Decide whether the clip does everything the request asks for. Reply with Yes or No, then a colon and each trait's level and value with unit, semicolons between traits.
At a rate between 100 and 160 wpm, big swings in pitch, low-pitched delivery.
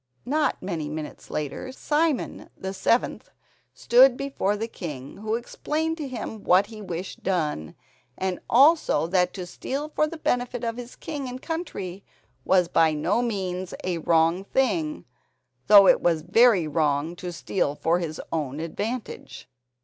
No: average, 150 wpm; wide, 6.9 semitones; high, 190 Hz